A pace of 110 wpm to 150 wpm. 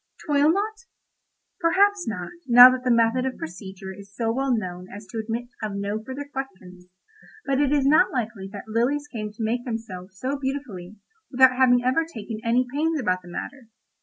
No: average, 180 wpm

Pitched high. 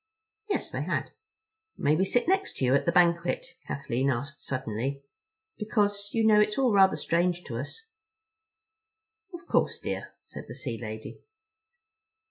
No: medium, 170 Hz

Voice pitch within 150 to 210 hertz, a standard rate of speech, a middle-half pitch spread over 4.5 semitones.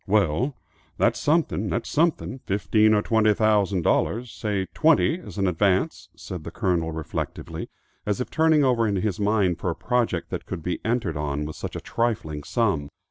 No: low, 105 Hz; average, 175 wpm; average, 5.1 semitones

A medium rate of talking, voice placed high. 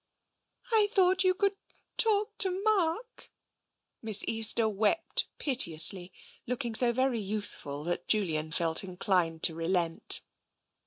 No: slow, 120 wpm; high, 220 Hz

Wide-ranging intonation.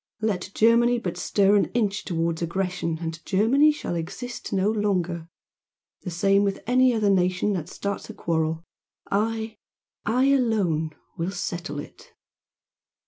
No: average, 4.6 semitones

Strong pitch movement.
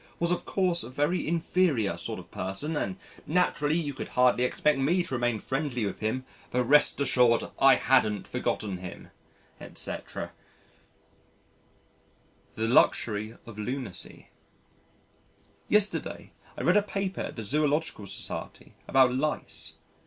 Yes: wide, 6.1 semitones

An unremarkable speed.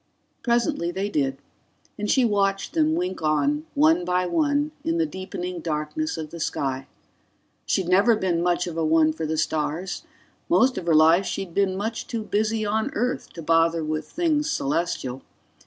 Yes: average, 170 wpm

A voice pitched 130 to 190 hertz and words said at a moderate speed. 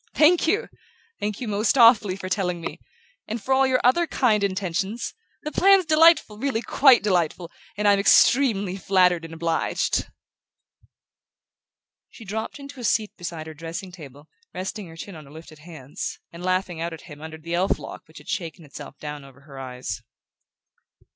Yes: medium, 185 Hz; average, 175 wpm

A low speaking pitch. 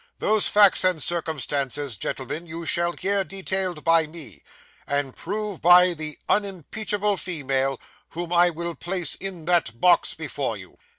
No: medium, 170 Hz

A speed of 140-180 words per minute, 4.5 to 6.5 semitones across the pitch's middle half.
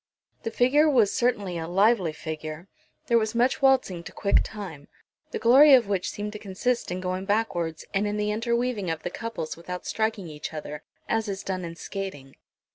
No: average, 190 wpm; average, 4.9 semitones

